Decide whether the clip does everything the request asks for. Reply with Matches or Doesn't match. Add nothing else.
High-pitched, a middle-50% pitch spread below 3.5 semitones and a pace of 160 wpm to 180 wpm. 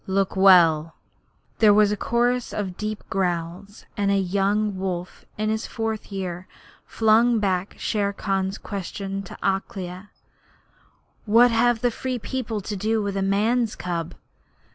Doesn't match